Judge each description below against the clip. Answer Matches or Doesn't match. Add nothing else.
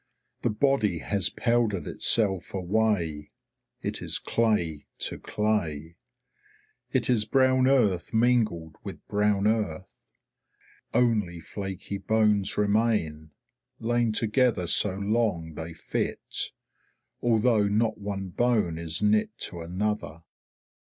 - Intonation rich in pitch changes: Doesn't match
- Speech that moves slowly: Matches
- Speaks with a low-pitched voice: Matches